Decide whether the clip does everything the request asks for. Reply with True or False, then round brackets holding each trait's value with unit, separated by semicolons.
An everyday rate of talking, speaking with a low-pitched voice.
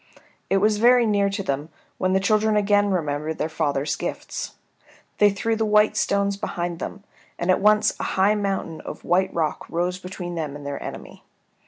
False (185 wpm; 190 Hz)